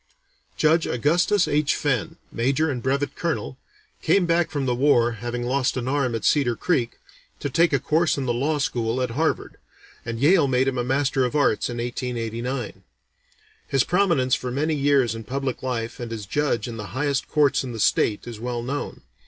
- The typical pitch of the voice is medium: No, low, 130 Hz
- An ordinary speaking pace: Yes, average, 190 wpm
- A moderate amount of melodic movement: Yes, average, 3.4 semitones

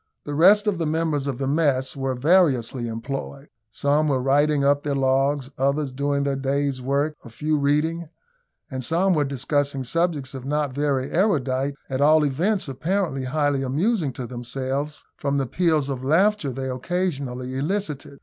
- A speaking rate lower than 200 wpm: Yes, average, 165 wpm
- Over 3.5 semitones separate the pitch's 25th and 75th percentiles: No, narrow, 2.6 semitones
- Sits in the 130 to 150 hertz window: Yes, medium, 140 Hz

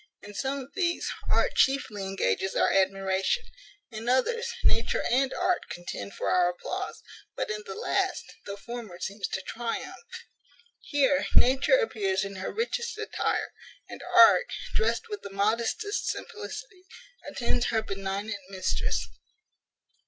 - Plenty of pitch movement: Yes, wide, 6.9 semitones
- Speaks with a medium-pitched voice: No, high, 225 Hz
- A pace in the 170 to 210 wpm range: No, slow, 135 wpm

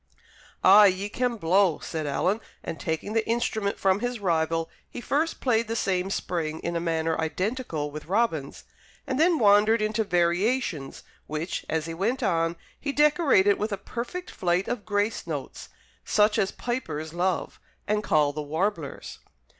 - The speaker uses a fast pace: No, average, 160 wpm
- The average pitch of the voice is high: Yes, high, 195 Hz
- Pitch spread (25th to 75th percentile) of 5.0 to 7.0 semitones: Yes, wide, 5.6 semitones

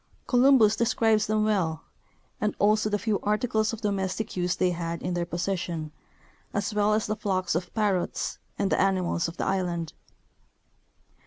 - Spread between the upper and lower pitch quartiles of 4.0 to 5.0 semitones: No, average, 3.3 semitones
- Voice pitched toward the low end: No, high, 200 Hz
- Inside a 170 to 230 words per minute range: No, average, 160 wpm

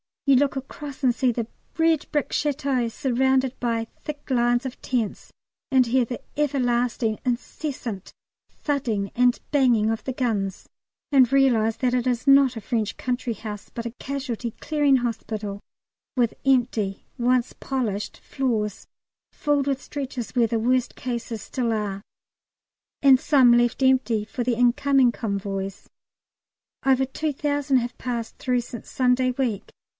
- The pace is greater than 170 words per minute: No, average, 145 wpm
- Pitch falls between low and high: No, very high, 250 Hz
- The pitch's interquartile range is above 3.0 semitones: No, average, 2.7 semitones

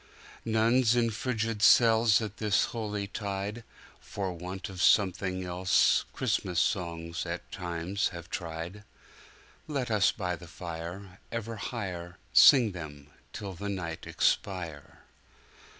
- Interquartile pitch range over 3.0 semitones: Yes, average, 3.9 semitones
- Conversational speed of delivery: No, slow, 115 wpm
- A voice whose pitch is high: No, very low, 95 Hz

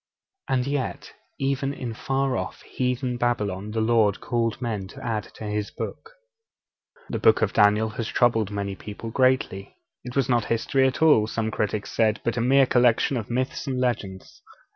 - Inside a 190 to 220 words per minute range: No, average, 175 wpm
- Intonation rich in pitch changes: No, average, 3.3 semitones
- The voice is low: Yes, low, 120 Hz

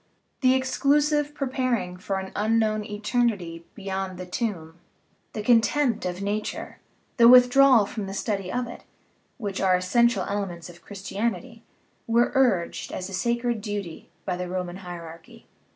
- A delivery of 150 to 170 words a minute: No, average, 140 wpm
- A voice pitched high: Yes, high, 205 Hz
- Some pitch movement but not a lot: Yes, average, 4.6 semitones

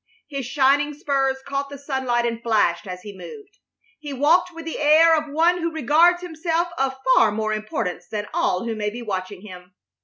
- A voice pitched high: Yes, very high, 270 Hz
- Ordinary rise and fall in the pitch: No, wide, 6.6 semitones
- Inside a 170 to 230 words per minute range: Yes, average, 190 wpm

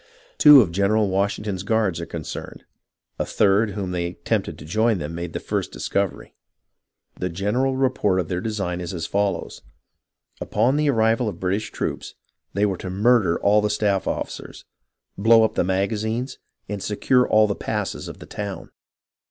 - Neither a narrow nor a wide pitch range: Yes, average, 3.2 semitones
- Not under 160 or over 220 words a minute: Yes, average, 170 wpm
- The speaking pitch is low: Yes, low, 100 Hz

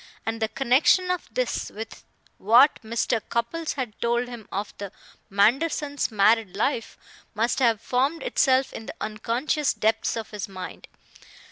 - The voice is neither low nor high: No, high, 235 Hz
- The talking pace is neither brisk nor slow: Yes, average, 145 wpm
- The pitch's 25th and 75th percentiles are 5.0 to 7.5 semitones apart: No, average, 3.7 semitones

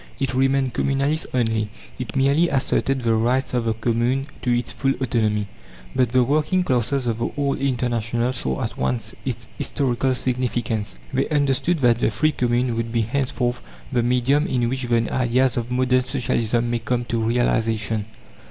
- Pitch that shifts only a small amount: Yes, narrow, 2.3 semitones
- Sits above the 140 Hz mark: No, low, 125 Hz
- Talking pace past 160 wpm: Yes, average, 170 wpm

